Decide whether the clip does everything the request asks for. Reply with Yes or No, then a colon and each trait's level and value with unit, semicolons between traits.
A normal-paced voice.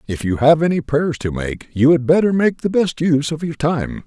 No: fast, 250 wpm